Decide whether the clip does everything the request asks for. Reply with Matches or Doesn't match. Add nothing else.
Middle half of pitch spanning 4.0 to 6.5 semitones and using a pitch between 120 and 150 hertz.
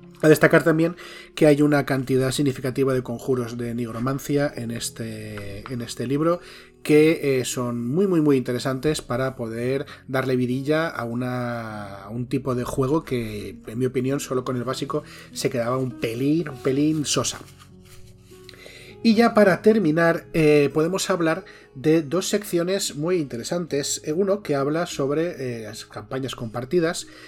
Matches